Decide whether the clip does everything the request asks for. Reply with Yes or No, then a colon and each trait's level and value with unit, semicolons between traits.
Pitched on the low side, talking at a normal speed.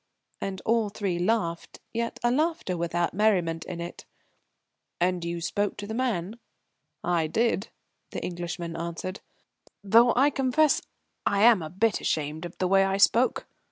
No: high, 195 Hz; average, 150 wpm